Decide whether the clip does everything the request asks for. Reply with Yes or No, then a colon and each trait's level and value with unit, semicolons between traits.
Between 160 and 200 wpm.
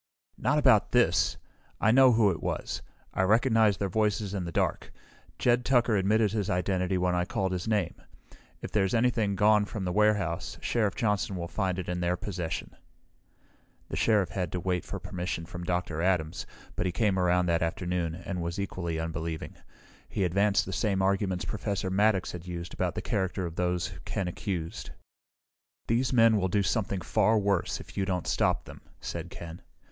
Yes: average, 180 wpm